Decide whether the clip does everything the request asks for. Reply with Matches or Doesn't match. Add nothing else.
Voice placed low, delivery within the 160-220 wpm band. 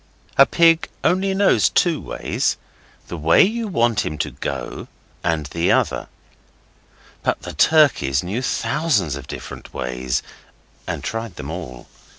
Doesn't match